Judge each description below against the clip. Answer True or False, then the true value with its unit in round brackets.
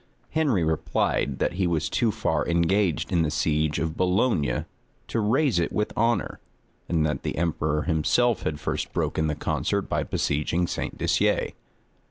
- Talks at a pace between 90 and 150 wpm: False (160 wpm)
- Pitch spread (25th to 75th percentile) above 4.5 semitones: True (5.2 semitones)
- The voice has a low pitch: True (85 Hz)